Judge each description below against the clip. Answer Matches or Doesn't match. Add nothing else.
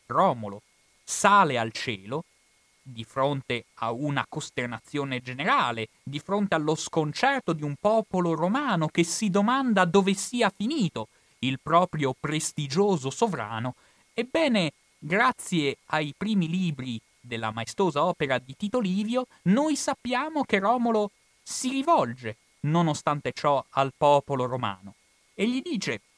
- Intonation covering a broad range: Matches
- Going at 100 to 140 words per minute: Matches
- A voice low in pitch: Doesn't match